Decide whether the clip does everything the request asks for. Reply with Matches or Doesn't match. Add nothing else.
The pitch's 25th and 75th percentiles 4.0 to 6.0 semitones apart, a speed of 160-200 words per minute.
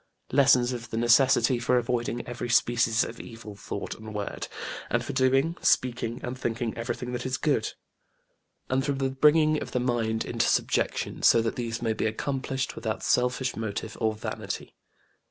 Doesn't match